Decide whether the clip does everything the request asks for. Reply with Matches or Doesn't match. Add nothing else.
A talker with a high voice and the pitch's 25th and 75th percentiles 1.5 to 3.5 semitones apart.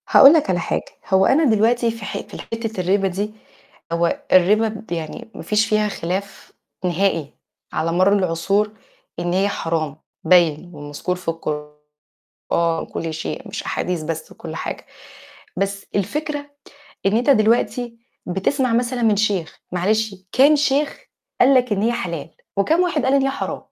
Doesn't match